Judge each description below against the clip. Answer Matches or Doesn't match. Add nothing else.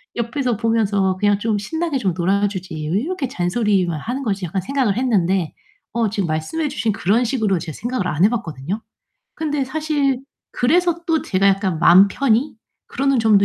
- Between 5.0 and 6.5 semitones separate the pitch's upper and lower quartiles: Matches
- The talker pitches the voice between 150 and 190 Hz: Doesn't match